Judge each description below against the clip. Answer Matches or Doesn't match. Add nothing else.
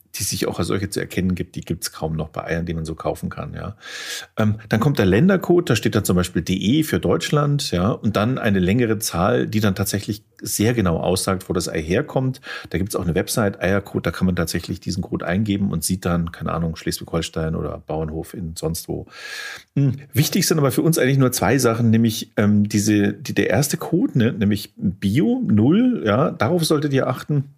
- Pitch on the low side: Matches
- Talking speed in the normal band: Doesn't match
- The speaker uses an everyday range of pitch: Doesn't match